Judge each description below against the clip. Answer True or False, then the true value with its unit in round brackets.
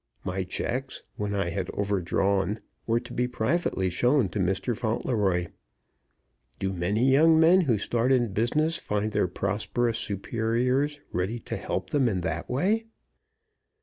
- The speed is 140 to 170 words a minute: True (145 wpm)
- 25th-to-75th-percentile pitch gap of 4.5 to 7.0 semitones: True (4.9 semitones)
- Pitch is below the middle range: True (110 Hz)